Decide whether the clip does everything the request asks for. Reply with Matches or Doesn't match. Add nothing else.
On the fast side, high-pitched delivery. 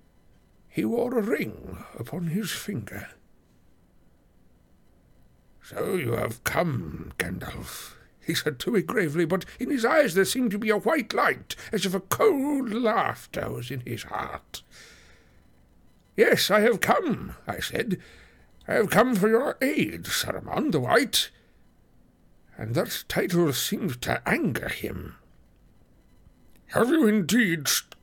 Doesn't match